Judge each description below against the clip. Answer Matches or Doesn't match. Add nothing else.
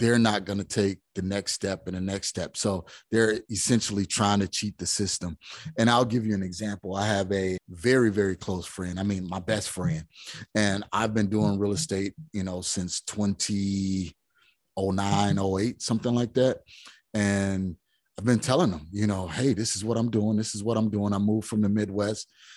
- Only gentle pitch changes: Matches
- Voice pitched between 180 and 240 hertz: Doesn't match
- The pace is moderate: Matches